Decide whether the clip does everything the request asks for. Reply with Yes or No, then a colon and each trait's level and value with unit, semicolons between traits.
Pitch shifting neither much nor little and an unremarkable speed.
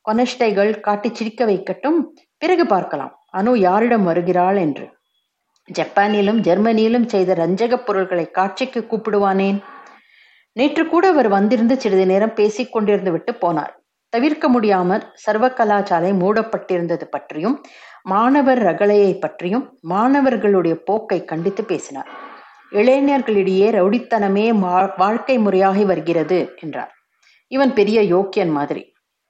Yes: average, 4.3 semitones; average, 100 wpm